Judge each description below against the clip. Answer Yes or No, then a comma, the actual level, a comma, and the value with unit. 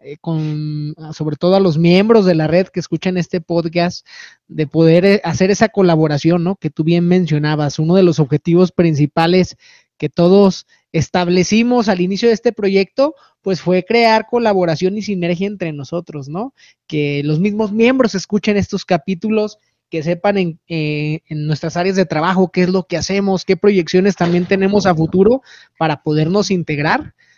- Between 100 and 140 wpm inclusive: No, average, 165 wpm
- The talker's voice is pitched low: No, medium, 180 Hz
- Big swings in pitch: No, average, 3.4 semitones